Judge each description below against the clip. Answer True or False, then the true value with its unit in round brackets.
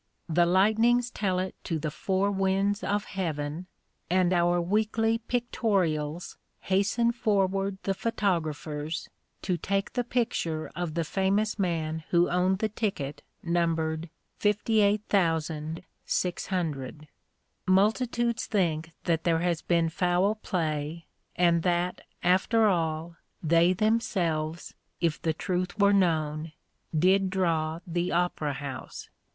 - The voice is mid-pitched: True (180 Hz)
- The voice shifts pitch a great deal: False (3.7 semitones)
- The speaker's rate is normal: False (115 wpm)